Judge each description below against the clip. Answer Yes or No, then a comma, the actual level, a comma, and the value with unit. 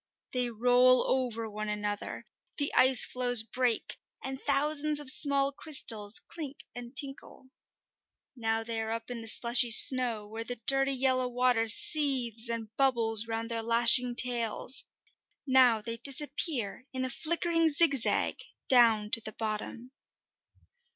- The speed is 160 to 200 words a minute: No, slow, 135 wpm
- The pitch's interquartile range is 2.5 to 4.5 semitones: Yes, average, 2.9 semitones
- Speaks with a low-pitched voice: No, high, 245 Hz